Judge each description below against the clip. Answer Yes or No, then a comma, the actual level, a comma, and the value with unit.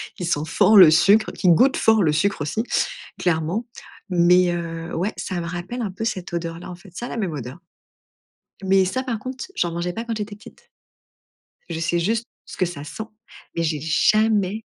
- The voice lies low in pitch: No, medium, 180 Hz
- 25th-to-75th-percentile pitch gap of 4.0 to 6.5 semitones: Yes, average, 4.4 semitones